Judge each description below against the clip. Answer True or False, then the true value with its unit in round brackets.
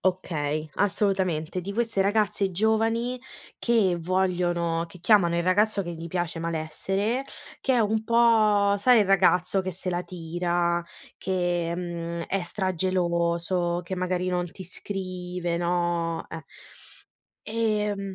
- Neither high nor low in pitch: True (180 Hz)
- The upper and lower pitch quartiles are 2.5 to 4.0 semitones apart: True (2.8 semitones)